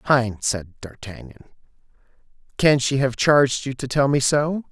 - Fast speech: No, average, 155 wpm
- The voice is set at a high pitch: No, low, 130 Hz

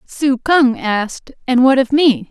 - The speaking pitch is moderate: No, very high, 260 Hz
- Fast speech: No, average, 180 wpm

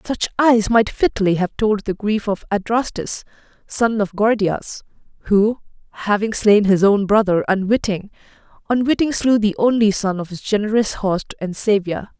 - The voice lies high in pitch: Yes, high, 210 Hz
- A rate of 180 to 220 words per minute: No, average, 155 wpm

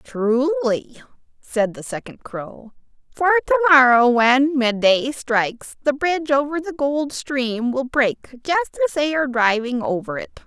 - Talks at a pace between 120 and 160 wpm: Yes, average, 150 wpm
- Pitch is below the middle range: No, very high, 270 Hz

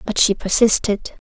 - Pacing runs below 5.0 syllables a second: Yes, 4.6 syllables/s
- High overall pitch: Yes, high, 210 Hz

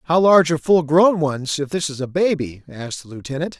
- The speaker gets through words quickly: Yes, fast, 235 wpm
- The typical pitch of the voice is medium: Yes, medium, 150 Hz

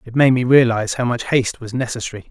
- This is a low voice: Yes, low, 120 Hz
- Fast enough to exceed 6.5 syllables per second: Yes, 6.8 syllables/s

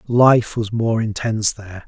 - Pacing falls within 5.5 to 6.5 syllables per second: No, 4.7 syllables/s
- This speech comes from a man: Yes, male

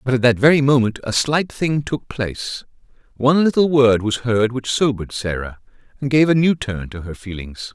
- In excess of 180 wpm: Yes, average, 200 wpm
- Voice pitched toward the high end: No, low, 125 Hz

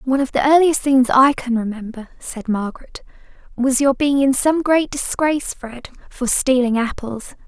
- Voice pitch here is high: Yes, very high, 260 Hz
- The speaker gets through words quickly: No, average, 170 wpm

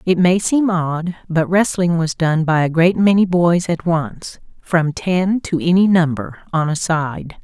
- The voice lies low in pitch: No, medium, 170 Hz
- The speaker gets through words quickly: No, average, 180 wpm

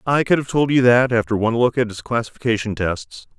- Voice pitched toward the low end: Yes, low, 120 Hz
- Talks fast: Yes, fast, 230 wpm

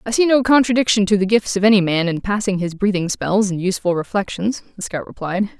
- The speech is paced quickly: Yes, fast, 225 wpm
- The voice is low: No, high, 200 Hz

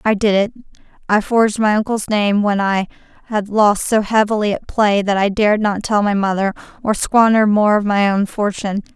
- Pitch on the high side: Yes, high, 210 Hz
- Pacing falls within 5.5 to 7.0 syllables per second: No, 5.1 syllables/s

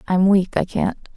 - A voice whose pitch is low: No, high, 190 Hz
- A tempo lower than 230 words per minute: Yes, fast, 205 wpm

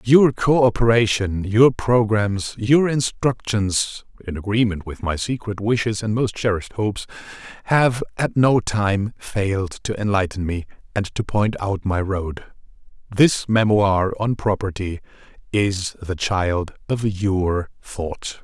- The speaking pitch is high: No, low, 105 Hz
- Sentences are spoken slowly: Yes, slow, 130 wpm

